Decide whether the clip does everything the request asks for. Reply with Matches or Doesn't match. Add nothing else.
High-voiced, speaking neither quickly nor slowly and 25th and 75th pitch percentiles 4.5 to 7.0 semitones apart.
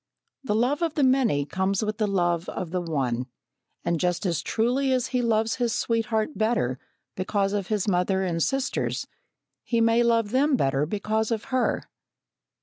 Matches